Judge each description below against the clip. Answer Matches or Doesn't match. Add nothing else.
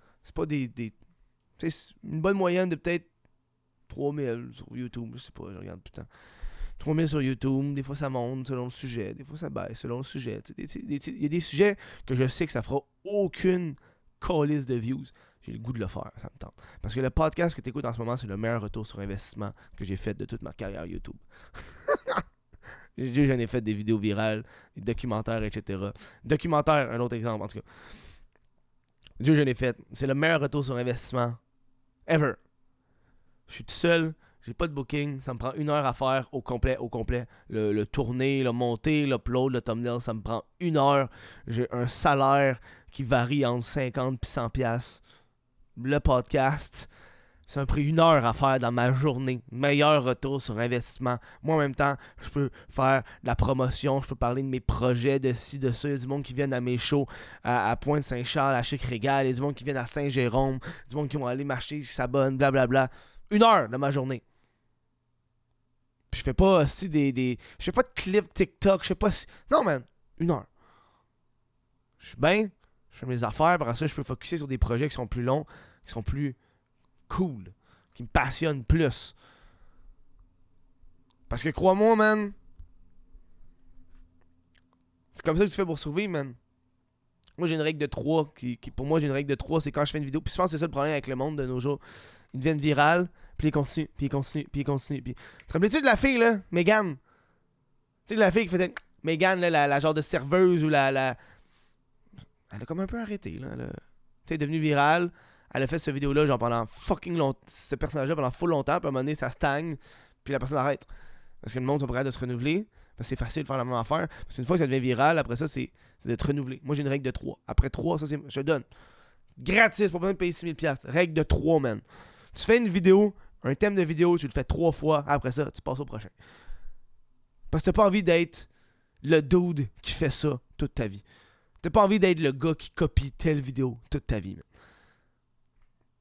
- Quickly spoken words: Matches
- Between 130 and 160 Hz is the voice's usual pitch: Matches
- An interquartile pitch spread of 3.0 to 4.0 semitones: Doesn't match